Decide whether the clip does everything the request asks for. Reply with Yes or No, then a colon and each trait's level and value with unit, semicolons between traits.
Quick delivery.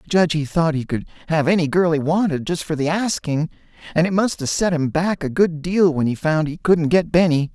Yes: fast, 255 wpm